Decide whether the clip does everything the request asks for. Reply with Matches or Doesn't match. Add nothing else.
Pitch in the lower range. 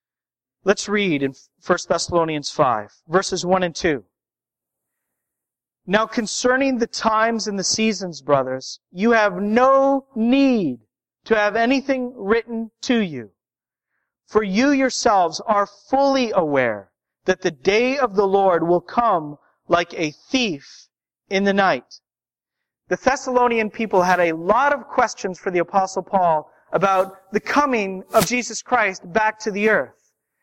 Doesn't match